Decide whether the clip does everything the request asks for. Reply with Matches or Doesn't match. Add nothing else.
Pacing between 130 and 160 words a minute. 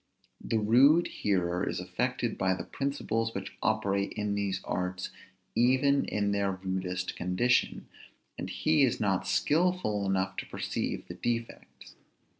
Matches